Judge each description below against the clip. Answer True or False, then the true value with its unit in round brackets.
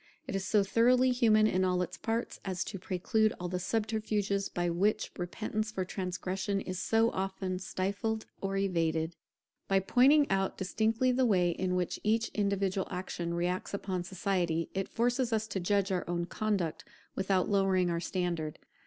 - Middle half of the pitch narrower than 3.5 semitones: True (3.0 semitones)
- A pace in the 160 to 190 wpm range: True (165 wpm)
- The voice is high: True (195 Hz)